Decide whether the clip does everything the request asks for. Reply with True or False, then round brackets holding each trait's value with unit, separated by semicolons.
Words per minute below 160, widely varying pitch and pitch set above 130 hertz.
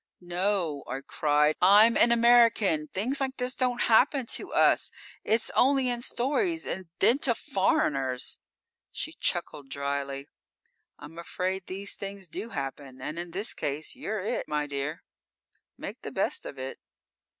True (150 wpm; 8.1 semitones; 190 Hz)